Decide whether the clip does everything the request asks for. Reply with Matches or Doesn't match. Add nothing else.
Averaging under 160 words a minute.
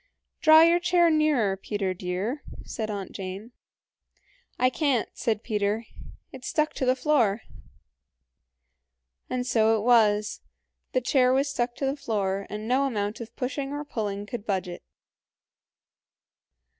Matches